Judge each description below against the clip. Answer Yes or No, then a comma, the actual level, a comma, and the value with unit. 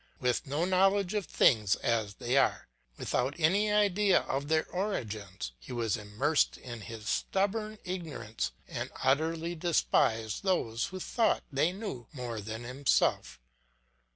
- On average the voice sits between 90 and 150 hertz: Yes, medium, 140 Hz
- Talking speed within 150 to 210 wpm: No, slow, 135 wpm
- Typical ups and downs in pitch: No, wide, 8.5 semitones